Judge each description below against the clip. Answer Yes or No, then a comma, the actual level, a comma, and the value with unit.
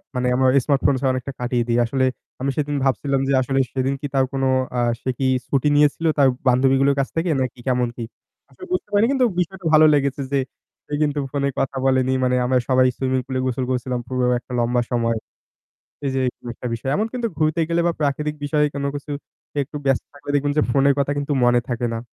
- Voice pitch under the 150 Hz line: Yes, low, 135 Hz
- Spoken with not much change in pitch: Yes, narrow, 2.3 semitones